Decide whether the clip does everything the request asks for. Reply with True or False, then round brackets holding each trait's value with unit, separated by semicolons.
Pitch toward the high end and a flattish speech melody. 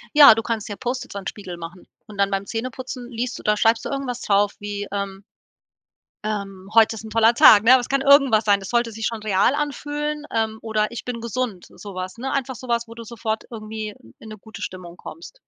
False (225 Hz; 3.2 semitones)